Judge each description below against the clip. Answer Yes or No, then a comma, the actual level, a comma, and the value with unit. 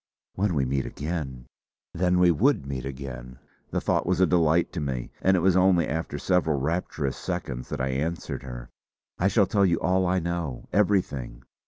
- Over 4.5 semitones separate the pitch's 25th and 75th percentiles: Yes, average, 5.3 semitones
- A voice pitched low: Yes, very low, 80 Hz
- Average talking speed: Yes, average, 185 wpm